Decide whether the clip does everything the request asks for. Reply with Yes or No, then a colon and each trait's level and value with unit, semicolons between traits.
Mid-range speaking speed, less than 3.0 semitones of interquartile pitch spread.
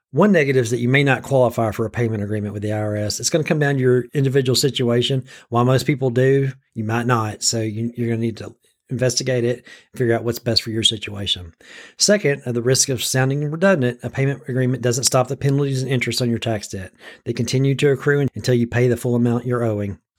No: fast, 235 wpm; narrow, 2.5 semitones